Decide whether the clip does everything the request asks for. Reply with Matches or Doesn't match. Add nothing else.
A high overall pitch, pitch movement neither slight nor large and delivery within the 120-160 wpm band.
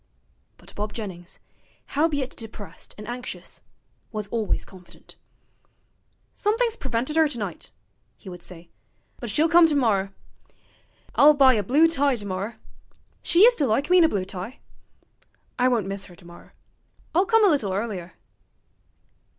Doesn't match